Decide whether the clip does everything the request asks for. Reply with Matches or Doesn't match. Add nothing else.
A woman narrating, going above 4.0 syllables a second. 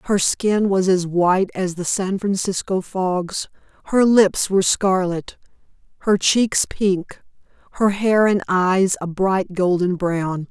Doesn't match